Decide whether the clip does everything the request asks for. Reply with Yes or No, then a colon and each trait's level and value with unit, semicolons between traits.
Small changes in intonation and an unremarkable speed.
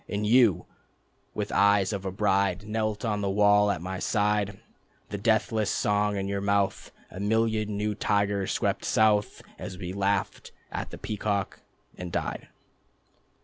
Yes: narrow, 1.2 semitones; average, 150 wpm